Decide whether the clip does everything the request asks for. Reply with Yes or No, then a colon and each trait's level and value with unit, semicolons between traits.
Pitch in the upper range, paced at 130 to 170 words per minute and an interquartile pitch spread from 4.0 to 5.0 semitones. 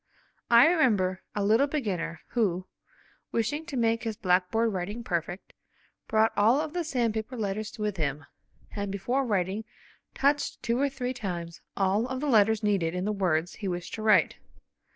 Yes: high, 215 Hz; average, 165 wpm; average, 4.7 semitones